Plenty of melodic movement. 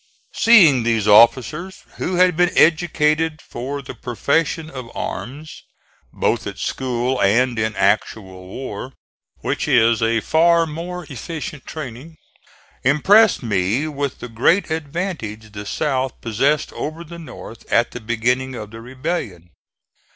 Yes: wide, 5.8 semitones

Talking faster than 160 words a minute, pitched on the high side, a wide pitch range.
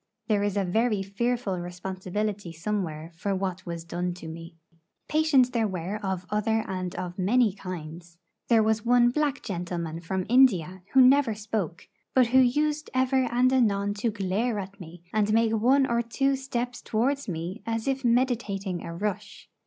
No: average, 170 wpm; high, 210 Hz; average, 5.0 semitones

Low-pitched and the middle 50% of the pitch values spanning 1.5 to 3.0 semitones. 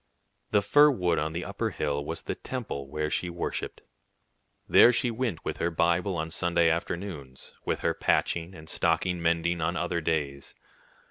Yes: very low, 85 Hz; narrow, 2.4 semitones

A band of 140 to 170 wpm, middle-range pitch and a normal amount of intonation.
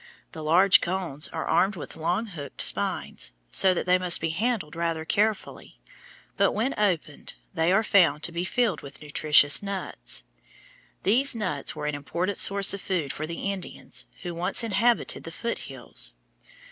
Yes: average, 165 wpm; medium, 180 Hz; average, 4.0 semitones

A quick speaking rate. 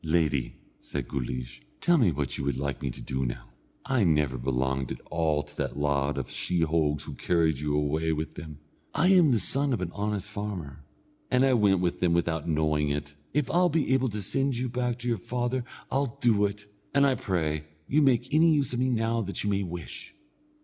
Yes: fast, 210 wpm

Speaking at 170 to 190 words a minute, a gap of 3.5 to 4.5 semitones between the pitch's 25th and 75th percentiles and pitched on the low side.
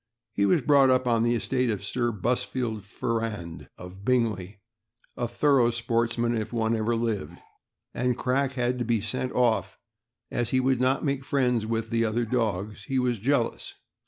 No: average, 180 wpm; narrow, 2.4 semitones; low, 120 Hz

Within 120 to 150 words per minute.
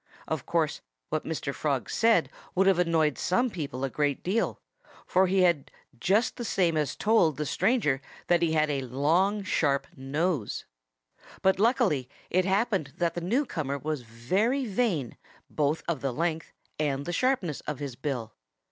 No: average, 165 wpm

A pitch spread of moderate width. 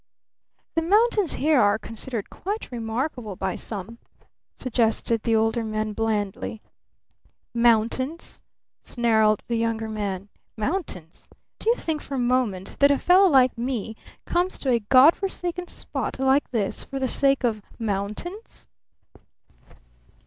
Yes: average, 4.7 semitones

